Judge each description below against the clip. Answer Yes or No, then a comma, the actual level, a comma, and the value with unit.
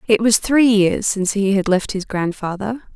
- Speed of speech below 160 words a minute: No, fast, 205 wpm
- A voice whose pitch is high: Yes, high, 205 Hz